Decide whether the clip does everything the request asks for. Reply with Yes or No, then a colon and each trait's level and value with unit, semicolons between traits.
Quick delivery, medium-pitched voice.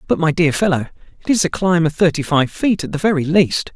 Yes: fast, 255 wpm; medium, 165 Hz